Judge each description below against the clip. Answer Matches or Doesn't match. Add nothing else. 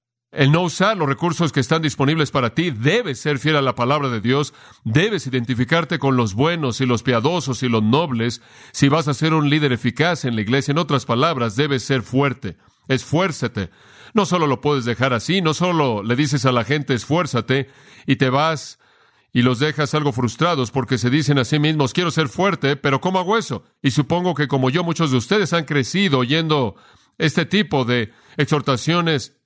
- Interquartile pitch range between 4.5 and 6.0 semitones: Doesn't match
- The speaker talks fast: Matches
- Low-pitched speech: Doesn't match